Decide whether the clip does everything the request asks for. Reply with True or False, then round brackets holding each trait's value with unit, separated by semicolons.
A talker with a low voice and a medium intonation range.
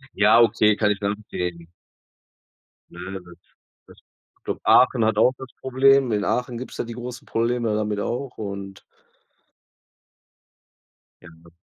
True (110 Hz; 3.5 semitones)